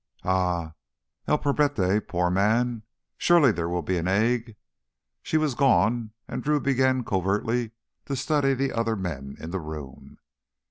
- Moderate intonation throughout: No, wide, 6.7 semitones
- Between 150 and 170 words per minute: No, slow, 135 wpm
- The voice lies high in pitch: No, low, 110 Hz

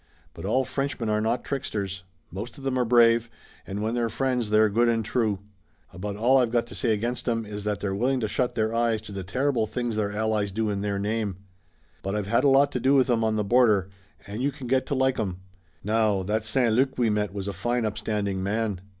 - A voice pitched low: Yes, low, 110 Hz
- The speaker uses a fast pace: Yes, fast, 235 wpm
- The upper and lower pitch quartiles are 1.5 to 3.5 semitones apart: Yes, average, 3.0 semitones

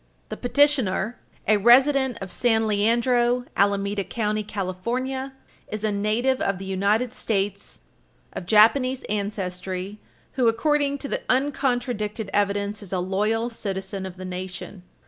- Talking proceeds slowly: Yes, slow, 130 wpm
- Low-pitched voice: No, high, 215 Hz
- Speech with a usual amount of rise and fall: Yes, average, 3.8 semitones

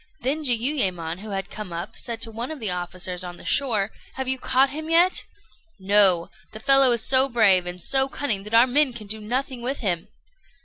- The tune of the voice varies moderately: No, wide, 5.7 semitones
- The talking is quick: Yes, fast, 210 wpm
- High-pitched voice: Yes, high, 225 Hz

